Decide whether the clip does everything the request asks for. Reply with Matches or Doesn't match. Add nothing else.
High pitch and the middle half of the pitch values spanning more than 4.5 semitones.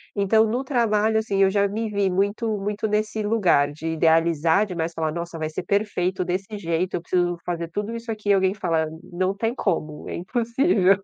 Doesn't match